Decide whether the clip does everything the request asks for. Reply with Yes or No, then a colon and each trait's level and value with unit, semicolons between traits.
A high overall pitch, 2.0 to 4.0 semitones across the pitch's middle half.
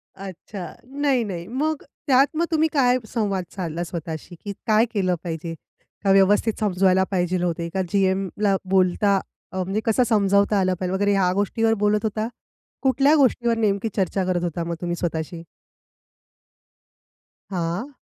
Yes: high, 195 Hz; average, 3.7 semitones